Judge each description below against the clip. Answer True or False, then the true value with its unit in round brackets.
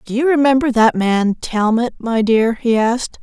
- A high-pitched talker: True (235 Hz)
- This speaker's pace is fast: False (185 wpm)